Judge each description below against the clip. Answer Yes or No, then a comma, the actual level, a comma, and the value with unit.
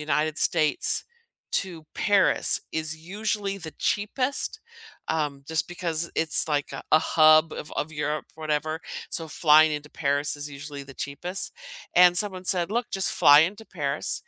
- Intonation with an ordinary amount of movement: Yes, average, 3.4 semitones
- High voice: No, medium, 160 Hz